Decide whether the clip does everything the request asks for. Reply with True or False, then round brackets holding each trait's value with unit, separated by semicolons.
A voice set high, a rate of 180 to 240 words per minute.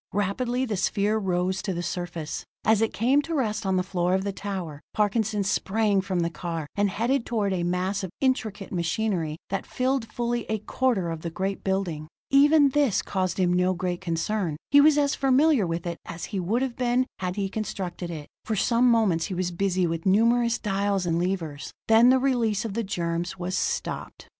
True (195 Hz; 200 wpm)